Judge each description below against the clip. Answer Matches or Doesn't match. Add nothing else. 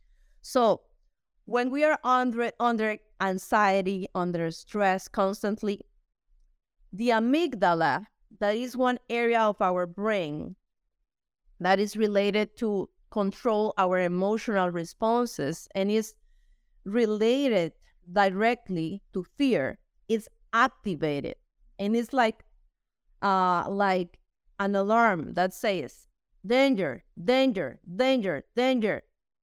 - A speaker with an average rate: Doesn't match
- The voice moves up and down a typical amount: Matches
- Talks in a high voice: Matches